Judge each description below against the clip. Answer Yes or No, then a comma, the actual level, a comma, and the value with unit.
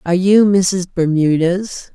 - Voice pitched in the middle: Yes, medium, 180 Hz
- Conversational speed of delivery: No, slow, 125 wpm